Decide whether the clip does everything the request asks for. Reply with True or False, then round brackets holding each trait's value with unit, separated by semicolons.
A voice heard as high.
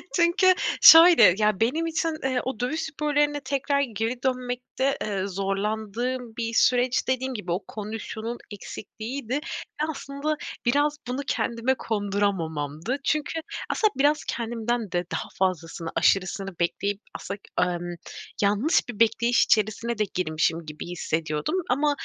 True (230 Hz)